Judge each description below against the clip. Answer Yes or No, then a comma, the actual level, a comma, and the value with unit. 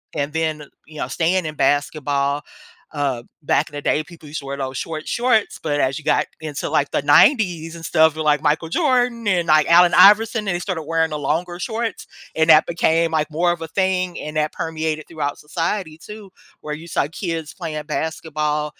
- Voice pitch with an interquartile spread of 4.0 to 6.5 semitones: No, narrow, 2.6 semitones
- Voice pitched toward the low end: No, medium, 160 Hz